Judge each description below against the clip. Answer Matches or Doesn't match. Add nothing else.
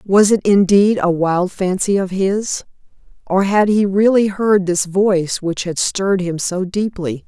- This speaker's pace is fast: Doesn't match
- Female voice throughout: Matches